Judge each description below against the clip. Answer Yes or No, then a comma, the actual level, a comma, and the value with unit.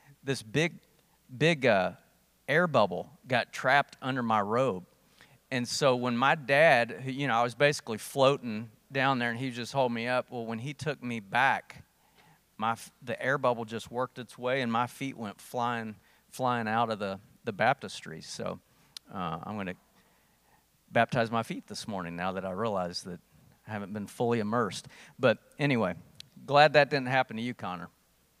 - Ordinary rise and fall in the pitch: Yes, average, 3.1 semitones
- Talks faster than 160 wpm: Yes, average, 175 wpm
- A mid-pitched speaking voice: No, low, 125 Hz